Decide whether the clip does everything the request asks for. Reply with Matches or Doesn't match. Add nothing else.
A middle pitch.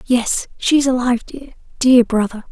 Doesn't match